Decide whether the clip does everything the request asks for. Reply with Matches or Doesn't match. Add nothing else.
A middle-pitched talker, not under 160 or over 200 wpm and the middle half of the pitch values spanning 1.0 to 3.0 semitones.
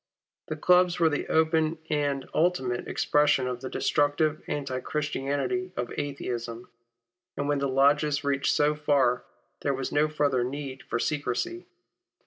Doesn't match